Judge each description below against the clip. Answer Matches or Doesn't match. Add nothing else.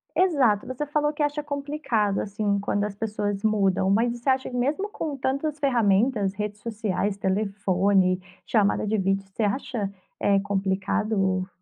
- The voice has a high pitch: Matches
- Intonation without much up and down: Doesn't match